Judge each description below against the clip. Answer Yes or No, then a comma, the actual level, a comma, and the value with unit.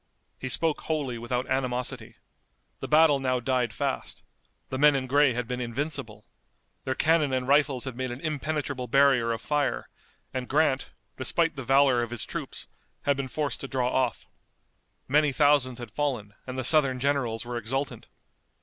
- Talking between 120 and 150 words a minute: No, average, 165 wpm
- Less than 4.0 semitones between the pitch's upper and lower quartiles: Yes, narrow, 2.6 semitones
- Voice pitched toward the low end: Yes, low, 130 Hz